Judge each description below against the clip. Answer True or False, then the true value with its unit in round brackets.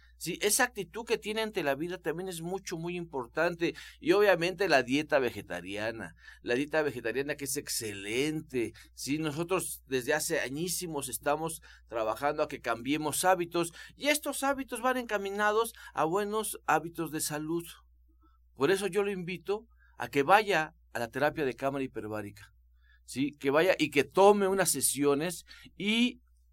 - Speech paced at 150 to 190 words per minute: True (155 wpm)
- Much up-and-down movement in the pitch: True (6.7 semitones)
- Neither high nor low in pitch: True (155 Hz)